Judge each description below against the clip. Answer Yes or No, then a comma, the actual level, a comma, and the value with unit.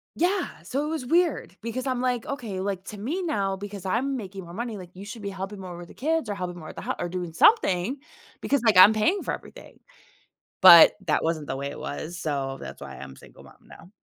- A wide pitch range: Yes, wide, 6.4 semitones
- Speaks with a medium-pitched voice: No, high, 200 Hz